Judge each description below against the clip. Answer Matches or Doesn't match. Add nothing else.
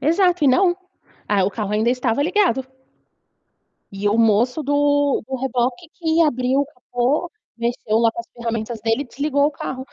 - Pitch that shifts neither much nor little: Matches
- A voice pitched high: Matches